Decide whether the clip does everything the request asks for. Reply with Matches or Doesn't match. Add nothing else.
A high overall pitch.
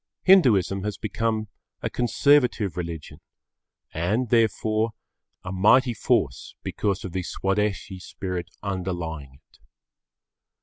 Doesn't match